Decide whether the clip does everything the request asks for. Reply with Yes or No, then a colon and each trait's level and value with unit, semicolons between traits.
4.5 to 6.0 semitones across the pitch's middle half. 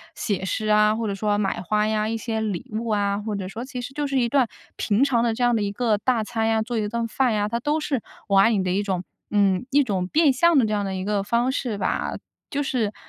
No: average, 3.1 semitones